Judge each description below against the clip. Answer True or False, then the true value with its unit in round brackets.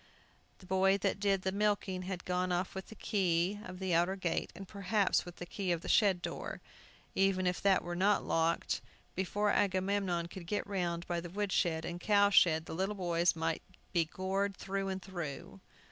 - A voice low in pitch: False (185 Hz)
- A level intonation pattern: True (2.2 semitones)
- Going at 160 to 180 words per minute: False (195 wpm)